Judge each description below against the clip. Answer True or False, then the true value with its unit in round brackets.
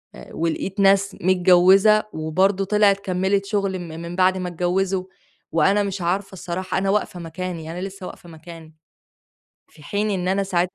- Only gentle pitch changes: True (2.0 semitones)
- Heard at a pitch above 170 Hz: True (185 Hz)